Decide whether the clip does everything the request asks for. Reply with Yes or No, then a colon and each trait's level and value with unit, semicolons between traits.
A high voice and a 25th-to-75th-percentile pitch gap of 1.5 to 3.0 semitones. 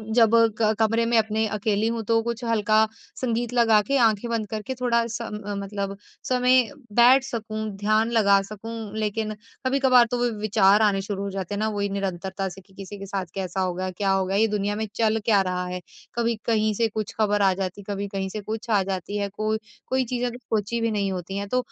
Yes: high, 215 Hz; narrow, 2.5 semitones